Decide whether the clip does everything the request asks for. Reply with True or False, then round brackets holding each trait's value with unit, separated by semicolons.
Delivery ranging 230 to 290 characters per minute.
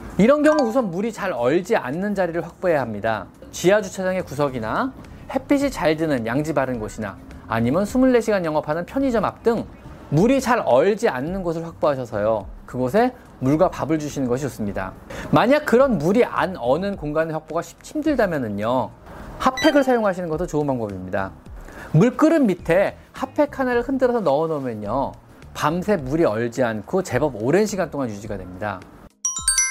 False (345 characters per minute)